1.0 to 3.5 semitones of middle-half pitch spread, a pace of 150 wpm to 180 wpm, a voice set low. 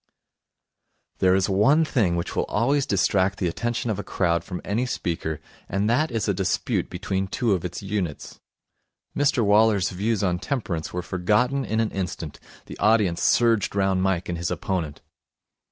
No: average, 3.9 semitones; average, 170 wpm; low, 100 Hz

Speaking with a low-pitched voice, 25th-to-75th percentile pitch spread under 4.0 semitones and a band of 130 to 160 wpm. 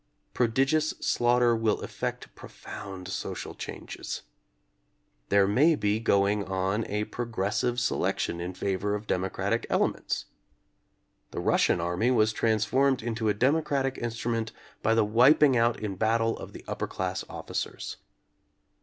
Yes: low, 110 Hz; average, 3.2 semitones; average, 140 wpm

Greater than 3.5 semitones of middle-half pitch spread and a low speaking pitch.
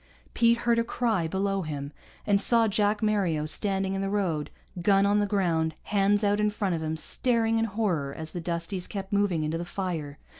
No: average, 4.0 semitones; high, 195 Hz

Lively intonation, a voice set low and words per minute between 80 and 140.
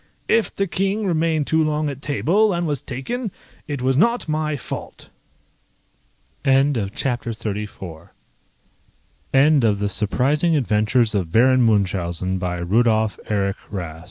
Yes: wide, 6.9 semitones; low, 130 Hz; slow, 135 wpm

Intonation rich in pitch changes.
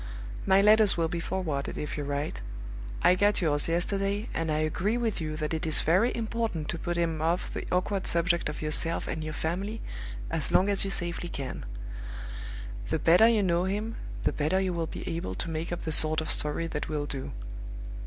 No: average, 3.9 semitones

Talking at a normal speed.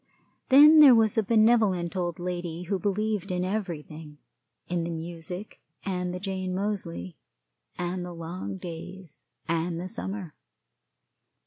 No: slow, 130 wpm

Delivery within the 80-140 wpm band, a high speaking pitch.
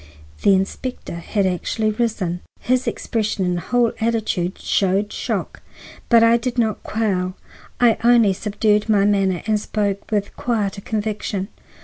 Yes: slow, 135 wpm; high, 210 Hz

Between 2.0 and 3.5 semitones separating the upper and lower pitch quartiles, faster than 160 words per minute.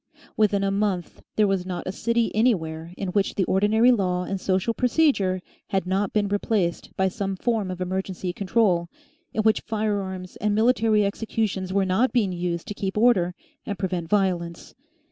Yes: average, 2.8 semitones; average, 170 wpm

